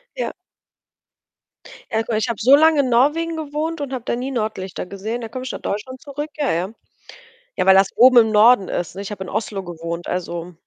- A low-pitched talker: No, high, 230 Hz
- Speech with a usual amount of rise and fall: No, wide, 6.0 semitones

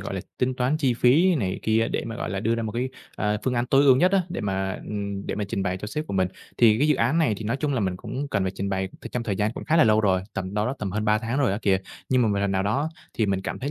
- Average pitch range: Yes, average, 4.6 semitones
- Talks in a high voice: No, low, 110 Hz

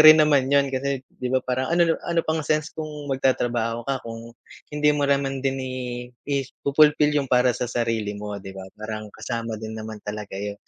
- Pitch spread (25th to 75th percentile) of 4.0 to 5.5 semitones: Yes, average, 4.3 semitones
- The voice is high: No, low, 130 Hz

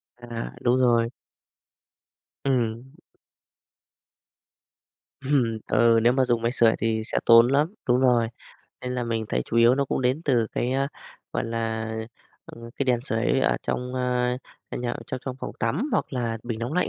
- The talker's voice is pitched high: No, low, 120 Hz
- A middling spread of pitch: No, narrow, 1.9 semitones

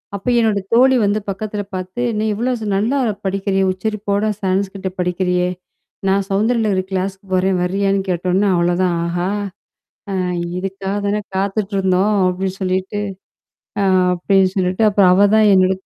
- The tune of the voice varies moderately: No, narrow, 1.7 semitones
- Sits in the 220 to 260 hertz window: No, high, 195 Hz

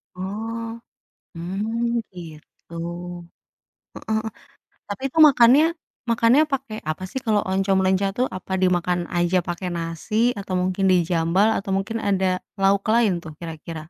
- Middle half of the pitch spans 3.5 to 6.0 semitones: Yes, average, 4.2 semitones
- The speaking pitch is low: No, high, 195 Hz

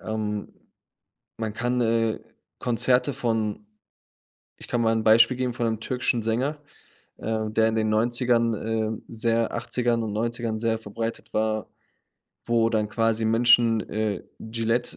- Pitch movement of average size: No, narrow, 1.2 semitones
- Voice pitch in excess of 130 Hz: No, low, 115 Hz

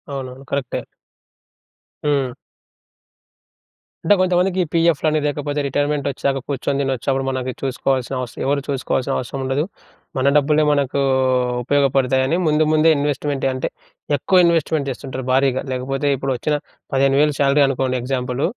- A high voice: No, medium, 140 Hz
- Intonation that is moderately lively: No, narrow, 2.0 semitones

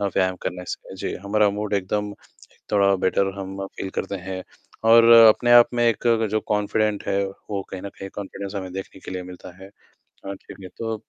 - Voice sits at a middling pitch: No, low, 100 Hz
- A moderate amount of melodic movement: No, narrow, 1.7 semitones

